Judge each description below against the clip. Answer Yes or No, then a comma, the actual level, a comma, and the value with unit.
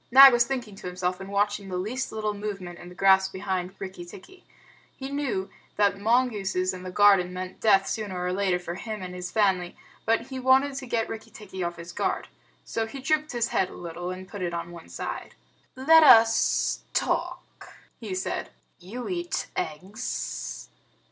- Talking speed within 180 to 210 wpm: Yes, average, 185 wpm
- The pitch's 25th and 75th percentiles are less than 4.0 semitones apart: No, average, 4.4 semitones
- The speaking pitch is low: No, high, 200 Hz